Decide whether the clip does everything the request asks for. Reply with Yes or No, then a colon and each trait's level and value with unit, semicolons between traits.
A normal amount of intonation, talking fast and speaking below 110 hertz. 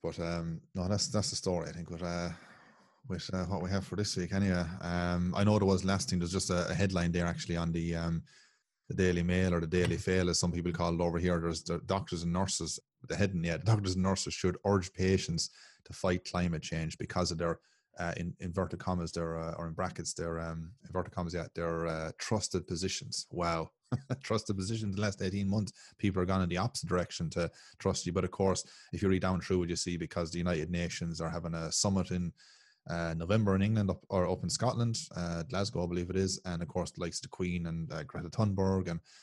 No: narrow, 2.1 semitones; fast, 240 wpm; very low, 90 Hz